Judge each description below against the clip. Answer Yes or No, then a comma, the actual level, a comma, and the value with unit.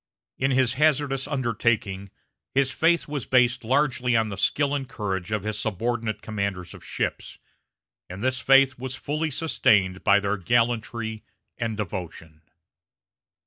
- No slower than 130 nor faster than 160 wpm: Yes, average, 140 wpm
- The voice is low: Yes, low, 120 Hz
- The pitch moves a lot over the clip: No, average, 4.5 semitones